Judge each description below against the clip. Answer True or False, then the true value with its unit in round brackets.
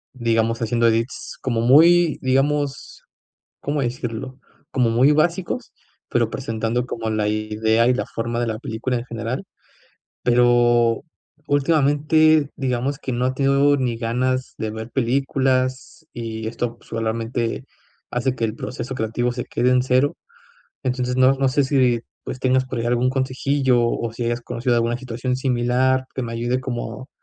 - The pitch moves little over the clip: True (2.2 semitones)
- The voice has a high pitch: False (125 Hz)